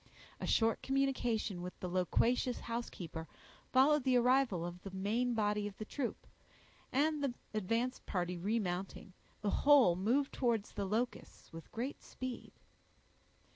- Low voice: No, high, 225 Hz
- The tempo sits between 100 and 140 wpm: Yes, slow, 135 wpm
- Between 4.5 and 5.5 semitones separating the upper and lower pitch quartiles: Yes, average, 5.1 semitones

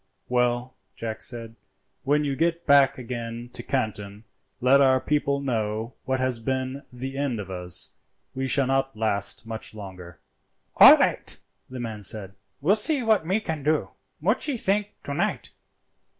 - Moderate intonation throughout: Yes, average, 4.1 semitones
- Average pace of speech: Yes, average, 155 wpm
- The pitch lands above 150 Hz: No, low, 130 Hz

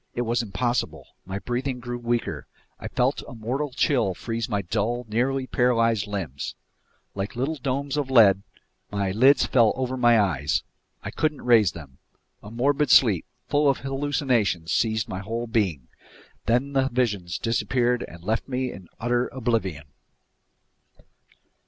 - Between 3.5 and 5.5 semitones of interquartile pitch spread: Yes, average, 4.1 semitones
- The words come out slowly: No, average, 145 wpm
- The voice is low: Yes, low, 120 Hz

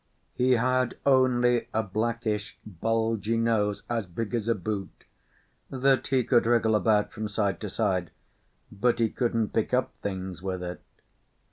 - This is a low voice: Yes, low, 110 Hz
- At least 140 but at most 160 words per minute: Yes, average, 150 wpm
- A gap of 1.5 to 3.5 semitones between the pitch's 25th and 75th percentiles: Yes, average, 2.7 semitones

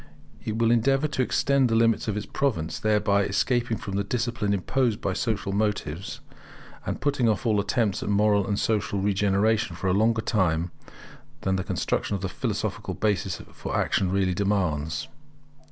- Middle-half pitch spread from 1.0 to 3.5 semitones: Yes, average, 2.8 semitones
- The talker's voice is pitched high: No, low, 105 Hz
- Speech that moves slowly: No, average, 170 wpm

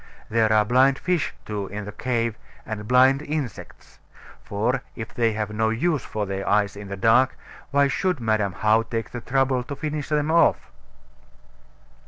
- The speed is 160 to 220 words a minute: Yes, average, 170 wpm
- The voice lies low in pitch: Yes, low, 115 Hz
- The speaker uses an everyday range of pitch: Yes, average, 4.2 semitones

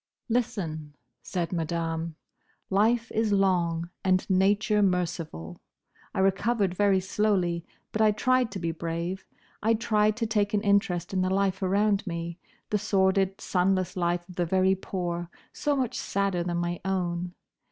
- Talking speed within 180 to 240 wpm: No, average, 150 wpm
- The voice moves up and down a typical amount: Yes, average, 3.0 semitones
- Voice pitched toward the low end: No, high, 190 Hz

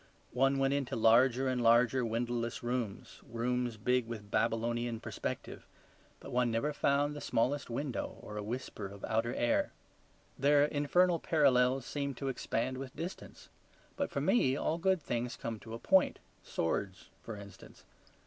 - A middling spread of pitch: Yes, average, 3.3 semitones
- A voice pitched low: Yes, low, 125 Hz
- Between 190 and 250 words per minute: No, average, 155 wpm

